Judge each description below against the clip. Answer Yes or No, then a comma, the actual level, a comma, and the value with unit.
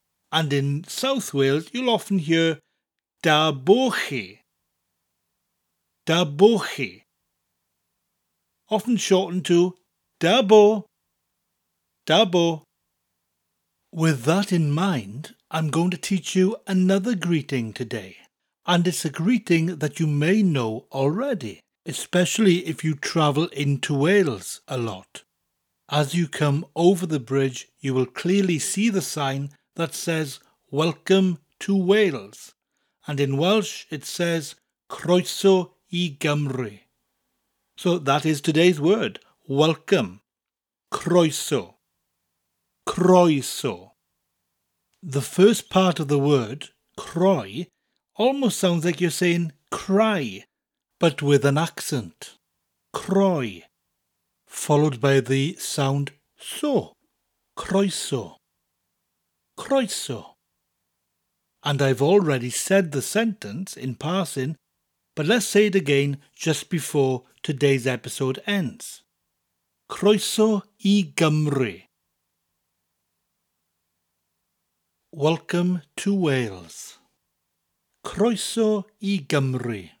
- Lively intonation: Yes, wide, 6.4 semitones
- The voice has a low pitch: No, medium, 155 Hz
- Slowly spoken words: Yes, slow, 95 wpm